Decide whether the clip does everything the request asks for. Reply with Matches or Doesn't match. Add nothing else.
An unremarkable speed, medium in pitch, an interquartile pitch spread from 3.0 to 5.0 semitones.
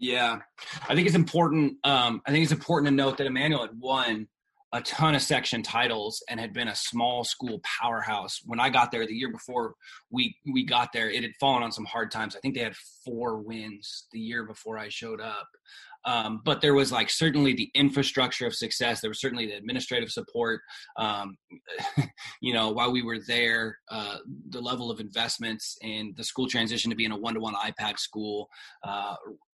Doesn't match